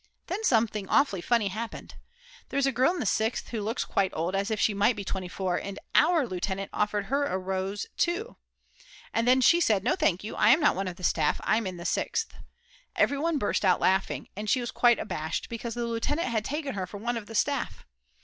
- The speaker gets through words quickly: Yes, fast, 225 wpm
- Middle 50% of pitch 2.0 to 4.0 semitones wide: No, average, 4.9 semitones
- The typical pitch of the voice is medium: No, high, 220 Hz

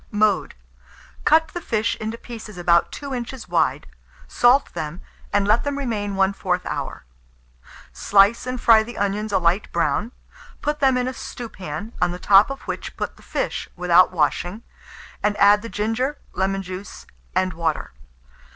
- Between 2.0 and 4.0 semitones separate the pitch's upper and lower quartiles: No, average, 4.4 semitones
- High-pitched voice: Yes, high, 210 Hz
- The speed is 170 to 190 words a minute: No, average, 160 wpm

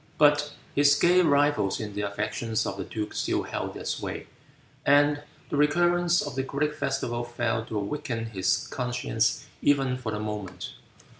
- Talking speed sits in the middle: Yes, average, 160 wpm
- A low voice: Yes, low, 125 Hz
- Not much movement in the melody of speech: No, average, 5.1 semitones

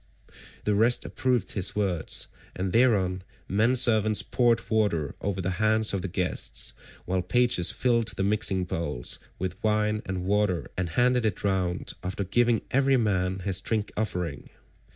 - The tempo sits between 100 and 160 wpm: Yes, average, 150 wpm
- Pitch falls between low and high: No, low, 100 Hz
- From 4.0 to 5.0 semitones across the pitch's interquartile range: No, average, 3.3 semitones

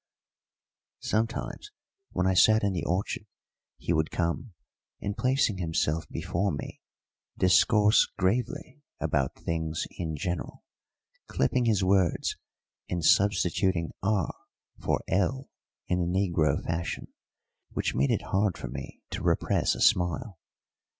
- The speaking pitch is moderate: No, very low, 95 Hz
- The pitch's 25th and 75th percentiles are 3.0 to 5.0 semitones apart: Yes, average, 3.8 semitones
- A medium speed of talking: No, slow, 125 wpm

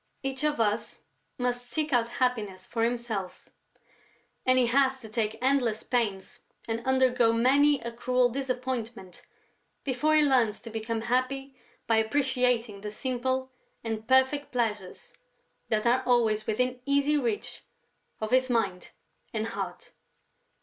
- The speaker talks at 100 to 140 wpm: Yes, slow, 135 wpm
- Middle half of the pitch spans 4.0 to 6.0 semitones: No, average, 2.7 semitones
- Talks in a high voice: Yes, high, 245 Hz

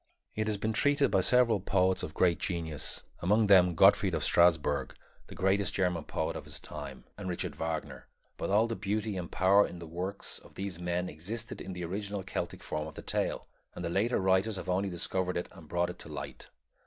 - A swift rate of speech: Yes, fast, 210 wpm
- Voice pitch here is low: Yes, very low, 95 Hz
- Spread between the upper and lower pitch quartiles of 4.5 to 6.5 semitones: No, average, 2.7 semitones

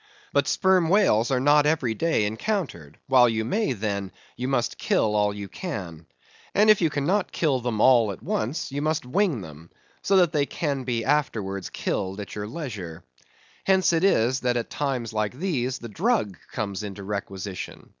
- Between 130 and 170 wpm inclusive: No, average, 180 wpm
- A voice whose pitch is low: Yes, low, 125 Hz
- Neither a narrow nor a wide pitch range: No, wide, 7.1 semitones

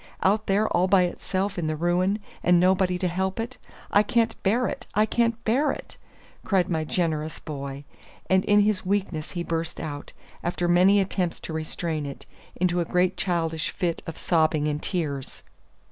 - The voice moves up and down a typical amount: Yes, average, 3.5 semitones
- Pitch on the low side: No, medium, 180 Hz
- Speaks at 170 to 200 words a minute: Yes, average, 175 wpm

